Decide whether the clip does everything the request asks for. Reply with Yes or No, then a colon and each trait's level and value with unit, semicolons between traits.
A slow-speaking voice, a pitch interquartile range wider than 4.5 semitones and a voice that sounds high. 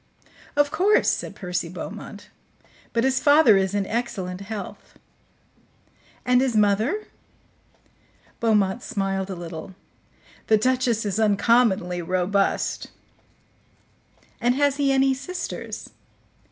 Yes: slow, 105 wpm; average, 5.1 semitones; high, 215 Hz